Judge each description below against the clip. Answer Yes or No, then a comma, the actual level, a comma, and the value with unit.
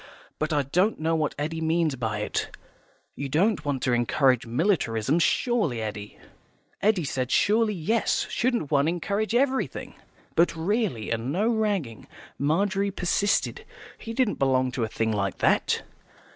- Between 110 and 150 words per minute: Yes, average, 145 wpm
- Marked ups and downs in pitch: Yes, wide, 8.0 semitones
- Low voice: No, medium, 160 Hz